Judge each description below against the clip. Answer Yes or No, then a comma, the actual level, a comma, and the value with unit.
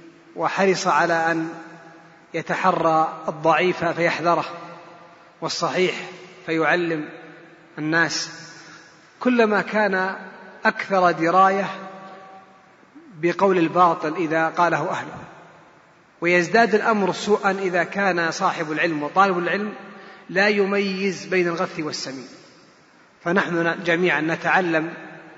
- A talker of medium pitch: Yes, medium, 175 Hz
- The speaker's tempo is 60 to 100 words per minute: Yes, average, 85 wpm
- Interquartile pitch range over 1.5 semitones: Yes, narrow, 2.5 semitones